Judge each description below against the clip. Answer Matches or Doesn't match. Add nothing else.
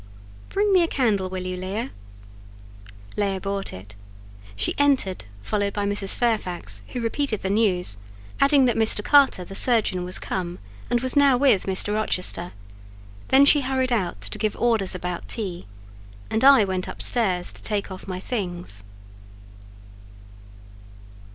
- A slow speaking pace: Doesn't match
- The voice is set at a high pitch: Matches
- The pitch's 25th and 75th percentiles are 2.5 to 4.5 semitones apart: Doesn't match